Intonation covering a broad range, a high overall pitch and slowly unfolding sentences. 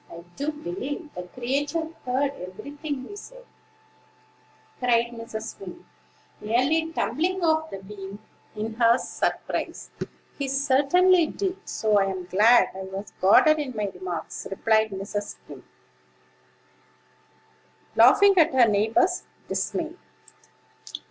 Yes: wide, 7.1 semitones; high, 245 Hz; slow, 115 wpm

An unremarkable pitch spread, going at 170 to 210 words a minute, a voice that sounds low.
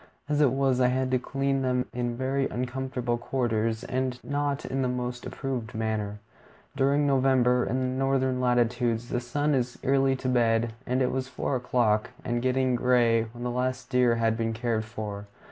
No: narrow, 1.8 semitones; average, 180 wpm; low, 125 Hz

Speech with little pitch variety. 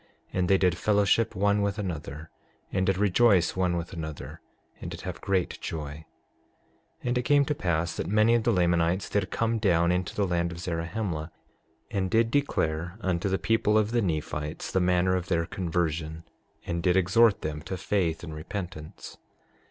No: average, 3.7 semitones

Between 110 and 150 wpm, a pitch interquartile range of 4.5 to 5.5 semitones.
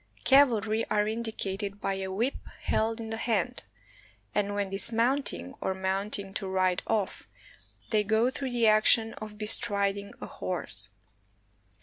No: average, 140 wpm; narrow, 2.4 semitones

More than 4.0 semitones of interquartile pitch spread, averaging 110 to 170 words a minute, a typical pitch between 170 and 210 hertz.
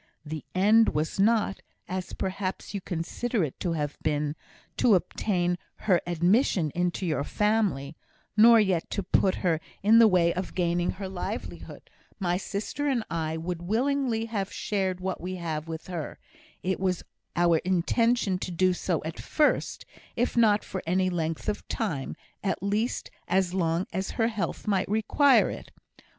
No: average, 3.6 semitones; average, 160 wpm; medium, 185 Hz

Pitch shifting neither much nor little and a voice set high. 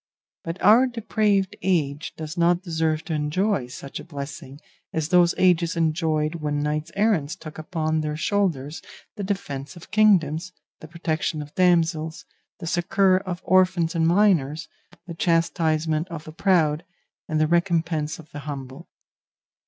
No: average, 3.0 semitones; medium, 165 Hz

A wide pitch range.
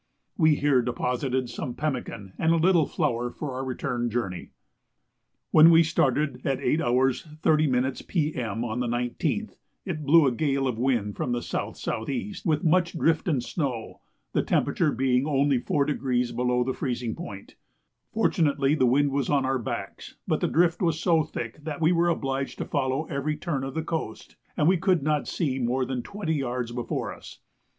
No: average, 4.2 semitones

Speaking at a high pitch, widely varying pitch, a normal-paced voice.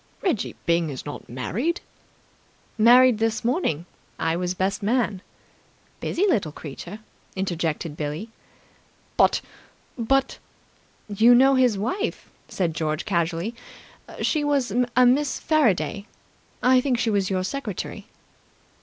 No: high, 215 Hz; wide, 6.7 semitones; slow, 120 wpm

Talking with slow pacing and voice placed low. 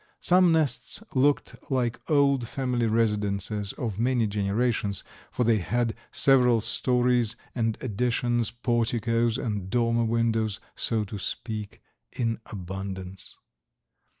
Yes: slow, 110 wpm; low, 115 Hz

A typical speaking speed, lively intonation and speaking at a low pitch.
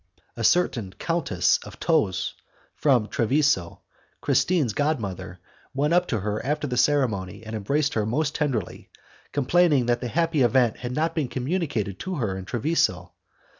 Yes: average, 155 wpm; wide, 6.1 semitones; low, 130 Hz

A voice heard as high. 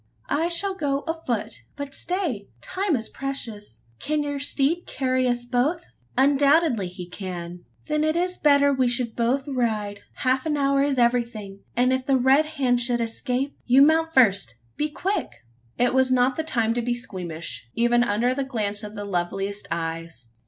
Yes: very high, 250 Hz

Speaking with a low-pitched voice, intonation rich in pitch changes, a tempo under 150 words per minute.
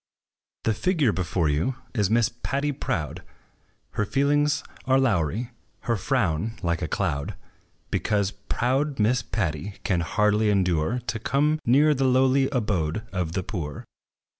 Yes: low, 110 Hz; wide, 6.9 semitones; average, 140 wpm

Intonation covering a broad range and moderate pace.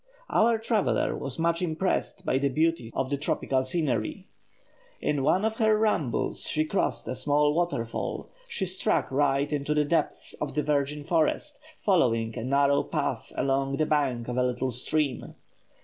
No: average, 4.1 semitones; average, 165 wpm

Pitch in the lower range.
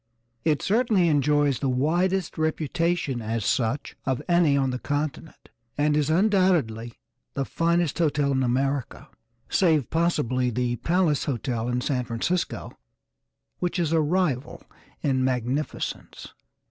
No: medium, 145 Hz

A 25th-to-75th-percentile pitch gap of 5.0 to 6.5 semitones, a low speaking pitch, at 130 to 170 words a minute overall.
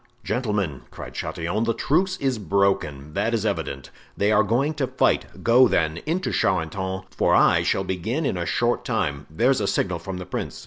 No: wide, 5.4 semitones; low, 100 Hz; average, 180 wpm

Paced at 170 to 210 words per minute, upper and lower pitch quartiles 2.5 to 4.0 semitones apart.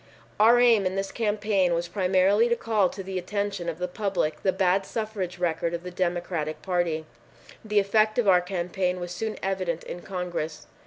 Yes: average, 180 wpm; average, 2.8 semitones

